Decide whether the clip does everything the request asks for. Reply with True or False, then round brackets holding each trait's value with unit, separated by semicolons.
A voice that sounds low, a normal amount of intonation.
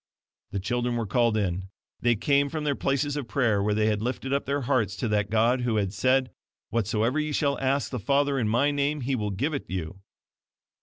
True (120 Hz; 4.7 semitones)